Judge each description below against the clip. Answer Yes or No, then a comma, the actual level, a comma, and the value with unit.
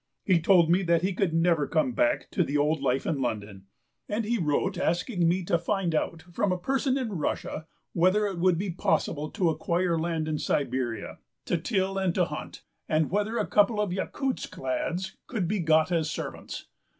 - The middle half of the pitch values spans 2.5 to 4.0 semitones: Yes, average, 3.7 semitones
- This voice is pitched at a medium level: Yes, medium, 175 Hz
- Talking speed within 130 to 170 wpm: No, average, 195 wpm